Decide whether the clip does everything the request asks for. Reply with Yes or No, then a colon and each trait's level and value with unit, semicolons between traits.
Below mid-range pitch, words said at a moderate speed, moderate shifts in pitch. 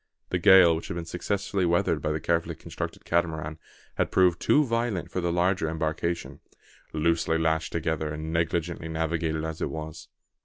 No: very low, 85 Hz; average, 165 wpm; narrow, 1.6 semitones